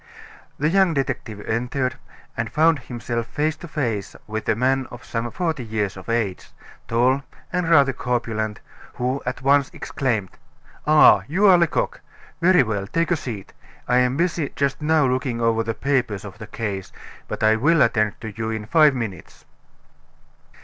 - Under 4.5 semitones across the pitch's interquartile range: No, average, 4.9 semitones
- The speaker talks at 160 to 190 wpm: Yes, average, 165 wpm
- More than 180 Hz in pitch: No, low, 125 Hz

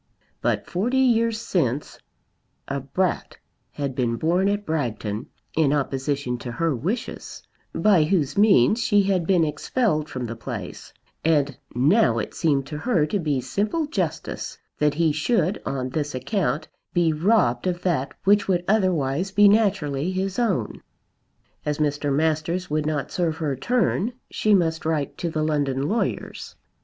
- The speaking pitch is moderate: Yes, medium, 160 Hz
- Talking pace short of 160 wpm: Yes, average, 150 wpm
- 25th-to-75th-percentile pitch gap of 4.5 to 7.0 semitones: Yes, wide, 5.6 semitones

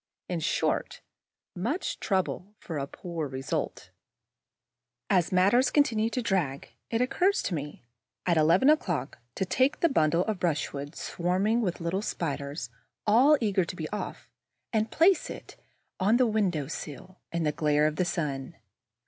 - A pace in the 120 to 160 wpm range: Yes, average, 155 wpm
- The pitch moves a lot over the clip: Yes, wide, 6.2 semitones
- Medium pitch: Yes, medium, 180 Hz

